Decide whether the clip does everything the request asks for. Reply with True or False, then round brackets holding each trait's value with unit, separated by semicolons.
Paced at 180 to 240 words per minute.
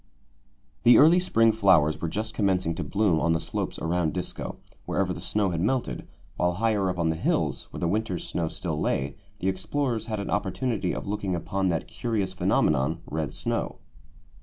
True (185 wpm)